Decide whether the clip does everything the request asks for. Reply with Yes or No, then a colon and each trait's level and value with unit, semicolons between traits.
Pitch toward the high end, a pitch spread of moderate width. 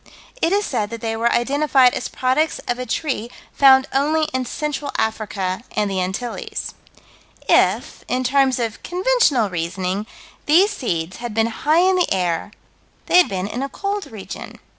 No: high, 245 Hz; wide, 6.1 semitones